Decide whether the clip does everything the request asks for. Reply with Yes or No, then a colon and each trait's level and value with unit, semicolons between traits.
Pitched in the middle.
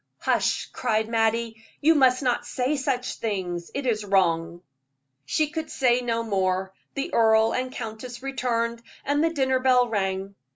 No: high, 235 Hz